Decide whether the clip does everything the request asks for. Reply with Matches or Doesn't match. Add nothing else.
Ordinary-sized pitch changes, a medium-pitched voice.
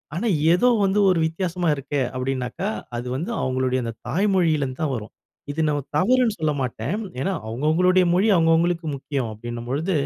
Doesn't match